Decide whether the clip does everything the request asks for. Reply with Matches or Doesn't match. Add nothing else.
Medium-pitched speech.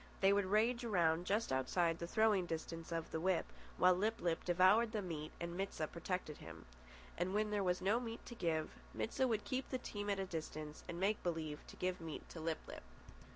Matches